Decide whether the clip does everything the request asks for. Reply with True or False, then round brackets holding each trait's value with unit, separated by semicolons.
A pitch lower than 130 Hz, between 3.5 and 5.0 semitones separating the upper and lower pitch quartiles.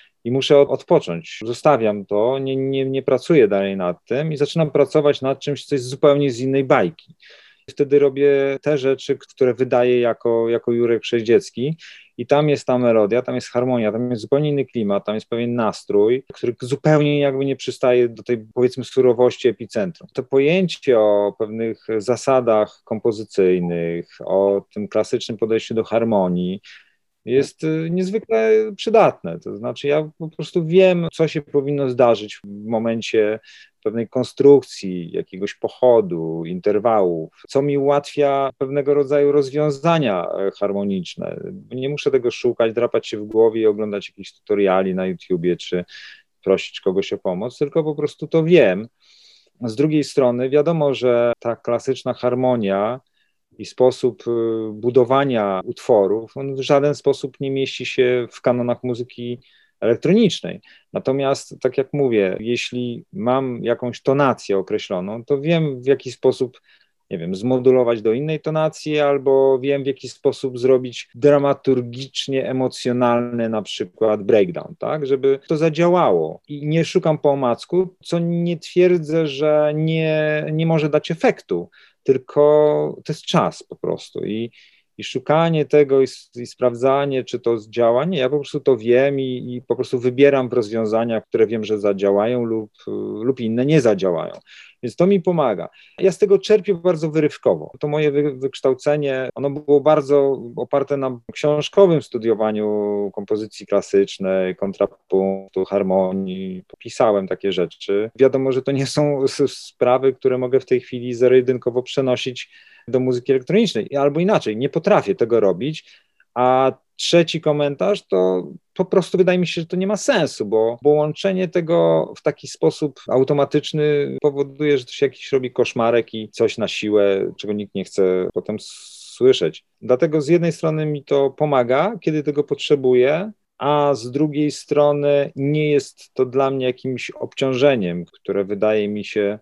False (135 Hz; 4.3 semitones)